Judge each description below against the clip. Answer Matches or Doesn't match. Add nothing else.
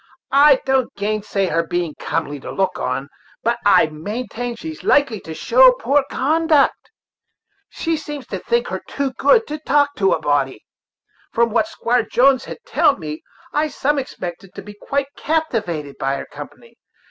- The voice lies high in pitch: Matches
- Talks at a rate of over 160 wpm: Matches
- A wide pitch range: Matches